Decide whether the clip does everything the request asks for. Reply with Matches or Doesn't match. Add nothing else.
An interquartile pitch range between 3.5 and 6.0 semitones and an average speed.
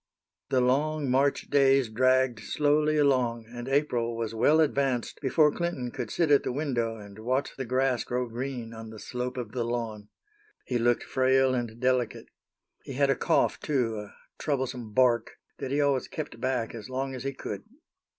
Doesn't match